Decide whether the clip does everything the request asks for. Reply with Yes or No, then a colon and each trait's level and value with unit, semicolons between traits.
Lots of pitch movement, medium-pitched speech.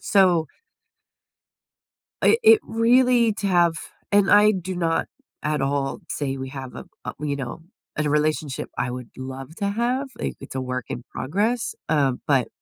Yes: wide, 7.3 semitones; medium, 155 Hz